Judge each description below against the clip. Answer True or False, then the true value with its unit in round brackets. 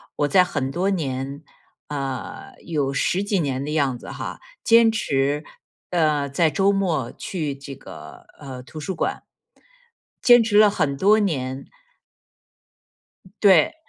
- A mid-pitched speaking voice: True (150 Hz)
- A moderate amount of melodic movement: False (5.9 semitones)